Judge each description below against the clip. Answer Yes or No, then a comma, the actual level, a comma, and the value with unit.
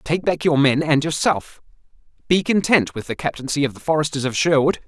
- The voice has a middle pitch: Yes, medium, 150 Hz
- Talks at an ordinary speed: Yes, average, 195 wpm